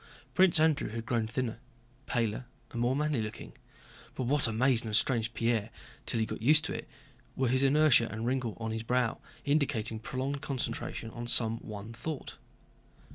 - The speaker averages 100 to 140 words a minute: No, average, 175 wpm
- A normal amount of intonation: Yes, average, 3.1 semitones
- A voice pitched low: Yes, low, 120 Hz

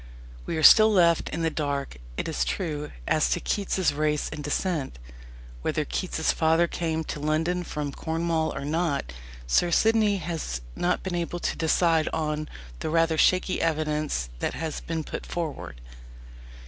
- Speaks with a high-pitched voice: No, medium, 160 Hz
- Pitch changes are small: Yes, narrow, 2.3 semitones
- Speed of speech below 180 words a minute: Yes, average, 160 wpm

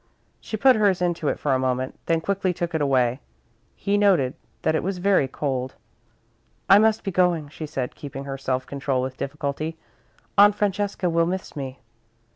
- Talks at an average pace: Yes, average, 180 wpm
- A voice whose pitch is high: No, medium, 160 Hz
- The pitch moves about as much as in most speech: No, wide, 6.0 semitones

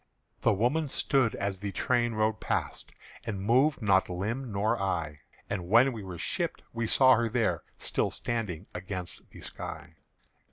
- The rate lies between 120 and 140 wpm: No, average, 160 wpm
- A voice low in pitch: Yes, low, 110 Hz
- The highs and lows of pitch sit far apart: No, average, 3.8 semitones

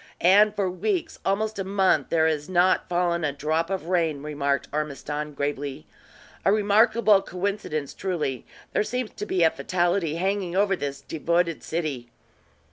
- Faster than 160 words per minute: No, average, 145 wpm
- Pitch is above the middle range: No, medium, 175 Hz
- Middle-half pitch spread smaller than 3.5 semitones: No, average, 4.5 semitones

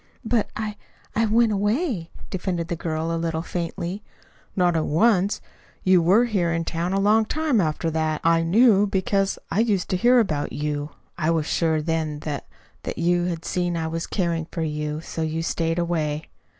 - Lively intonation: No, average, 3.6 semitones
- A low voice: No, medium, 170 Hz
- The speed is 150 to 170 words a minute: No, average, 190 wpm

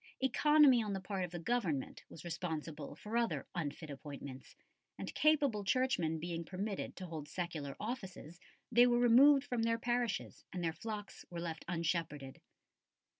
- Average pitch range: No, wide, 6.6 semitones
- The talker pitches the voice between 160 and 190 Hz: Yes, medium, 185 Hz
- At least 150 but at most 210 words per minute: Yes, average, 155 wpm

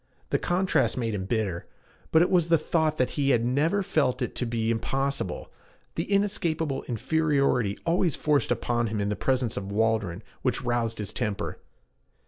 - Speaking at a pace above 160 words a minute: Yes, average, 170 wpm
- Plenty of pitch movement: Yes, wide, 6.2 semitones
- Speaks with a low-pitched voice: Yes, low, 125 Hz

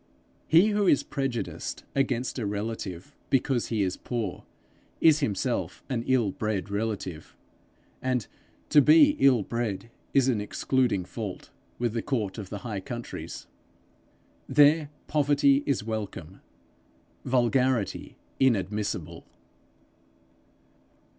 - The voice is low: Yes, low, 120 Hz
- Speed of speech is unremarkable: No, slow, 110 wpm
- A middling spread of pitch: Yes, average, 4.7 semitones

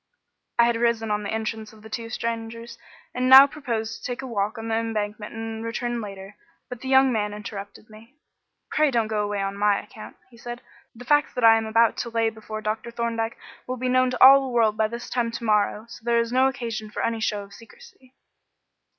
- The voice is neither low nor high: No, high, 230 Hz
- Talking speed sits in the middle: No, fast, 225 wpm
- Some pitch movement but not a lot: No, narrow, 2.0 semitones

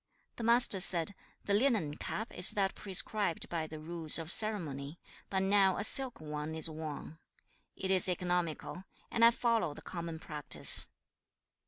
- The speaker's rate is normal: Yes, average, 155 wpm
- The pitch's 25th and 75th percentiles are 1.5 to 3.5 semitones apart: No, average, 4.5 semitones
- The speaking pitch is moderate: Yes, medium, 180 Hz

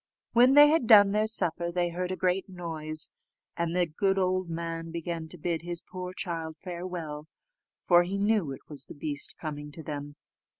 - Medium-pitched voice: Yes, medium, 175 Hz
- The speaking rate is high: No, average, 185 wpm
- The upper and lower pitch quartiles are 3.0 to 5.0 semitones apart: No, narrow, 2.6 semitones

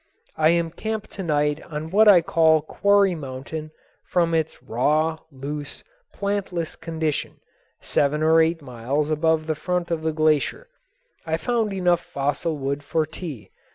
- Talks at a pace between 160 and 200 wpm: No, average, 150 wpm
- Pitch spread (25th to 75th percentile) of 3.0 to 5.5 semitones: No, narrow, 2.6 semitones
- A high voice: No, medium, 160 Hz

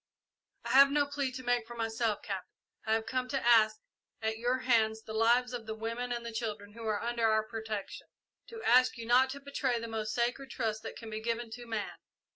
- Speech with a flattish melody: Yes, narrow, 2.1 semitones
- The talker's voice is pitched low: No, high, 230 Hz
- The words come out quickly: Yes, fast, 220 wpm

